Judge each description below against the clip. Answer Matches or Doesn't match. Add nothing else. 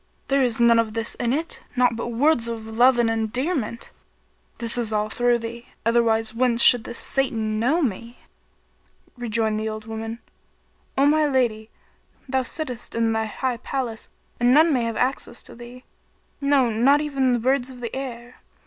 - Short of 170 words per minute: Doesn't match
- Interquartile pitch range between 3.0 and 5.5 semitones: Doesn't match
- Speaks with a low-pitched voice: Doesn't match